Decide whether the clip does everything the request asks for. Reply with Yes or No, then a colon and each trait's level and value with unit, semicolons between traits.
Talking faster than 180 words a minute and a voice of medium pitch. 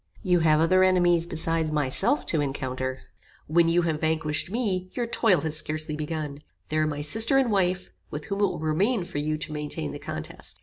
Yes: average, 200 wpm; medium, 160 Hz